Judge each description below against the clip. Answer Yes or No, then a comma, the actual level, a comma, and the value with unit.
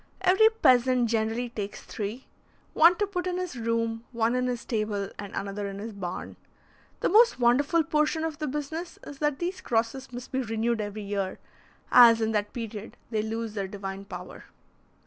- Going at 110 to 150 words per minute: No, average, 180 wpm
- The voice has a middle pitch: No, high, 230 Hz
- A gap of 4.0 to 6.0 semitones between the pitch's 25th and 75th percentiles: Yes, average, 5.3 semitones